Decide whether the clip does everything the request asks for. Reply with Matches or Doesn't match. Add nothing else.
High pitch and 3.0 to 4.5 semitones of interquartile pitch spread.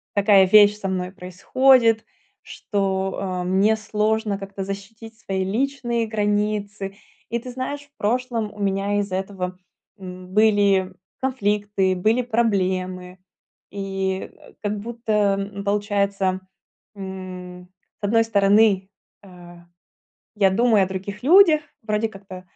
Doesn't match